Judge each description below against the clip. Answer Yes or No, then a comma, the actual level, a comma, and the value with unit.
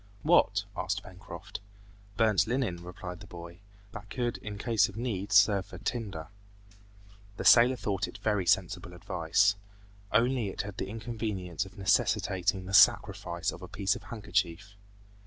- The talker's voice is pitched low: Yes, low, 100 Hz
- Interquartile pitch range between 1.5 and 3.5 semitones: Yes, average, 3.0 semitones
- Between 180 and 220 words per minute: No, average, 150 wpm